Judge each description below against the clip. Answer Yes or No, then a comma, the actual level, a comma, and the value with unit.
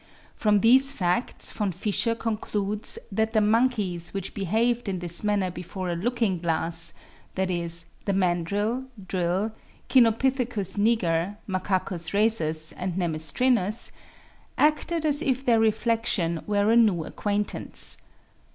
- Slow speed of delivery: Yes, slow, 120 wpm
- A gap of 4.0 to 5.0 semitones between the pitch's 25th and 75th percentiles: Yes, average, 4.3 semitones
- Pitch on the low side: No, high, 205 Hz